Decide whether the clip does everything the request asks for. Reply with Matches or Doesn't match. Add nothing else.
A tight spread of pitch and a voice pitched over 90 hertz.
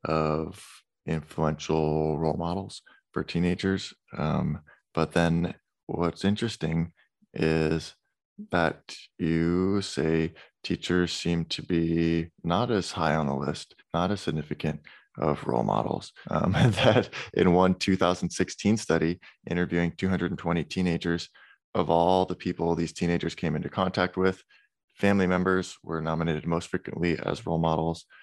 Doesn't match